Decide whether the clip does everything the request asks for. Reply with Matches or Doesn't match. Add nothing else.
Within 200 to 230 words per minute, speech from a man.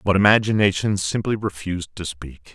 Doesn't match